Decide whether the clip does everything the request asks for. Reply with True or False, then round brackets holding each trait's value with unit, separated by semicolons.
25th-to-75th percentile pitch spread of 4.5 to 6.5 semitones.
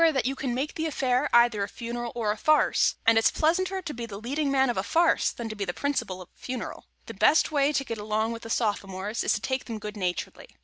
True (4.8 semitones)